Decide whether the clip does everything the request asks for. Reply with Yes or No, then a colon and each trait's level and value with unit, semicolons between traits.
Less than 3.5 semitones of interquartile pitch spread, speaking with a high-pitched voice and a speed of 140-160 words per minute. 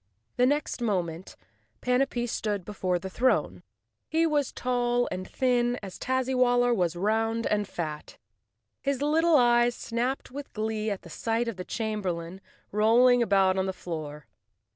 No: average, 4.7 semitones; high, 230 Hz; average, 145 wpm